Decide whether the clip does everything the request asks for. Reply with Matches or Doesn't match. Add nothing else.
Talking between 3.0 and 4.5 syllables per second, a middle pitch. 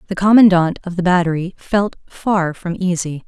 Doesn't match